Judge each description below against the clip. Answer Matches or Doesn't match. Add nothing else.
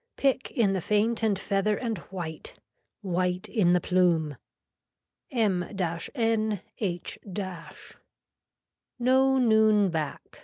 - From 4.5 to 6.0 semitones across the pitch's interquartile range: Doesn't match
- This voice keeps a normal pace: Doesn't match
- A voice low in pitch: Doesn't match